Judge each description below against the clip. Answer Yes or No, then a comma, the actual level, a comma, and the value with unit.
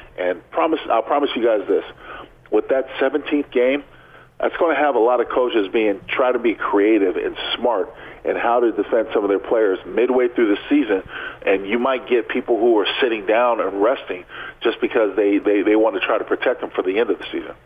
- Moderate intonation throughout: Yes, average, 4.0 semitones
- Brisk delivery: Yes, fast, 225 wpm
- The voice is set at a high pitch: Yes, very high, 390 Hz